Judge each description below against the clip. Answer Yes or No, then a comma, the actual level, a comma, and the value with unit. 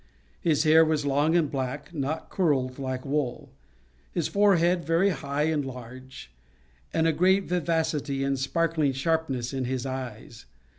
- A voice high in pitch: No, medium, 145 Hz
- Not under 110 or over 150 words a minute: Yes, average, 145 wpm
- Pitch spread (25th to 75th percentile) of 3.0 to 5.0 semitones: Yes, average, 3.6 semitones